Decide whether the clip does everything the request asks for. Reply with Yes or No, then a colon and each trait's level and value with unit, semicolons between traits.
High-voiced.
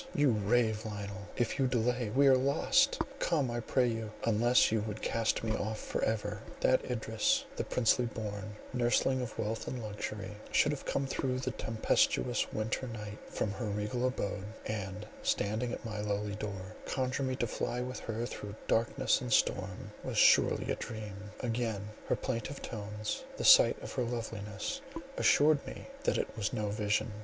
No: low, 110 Hz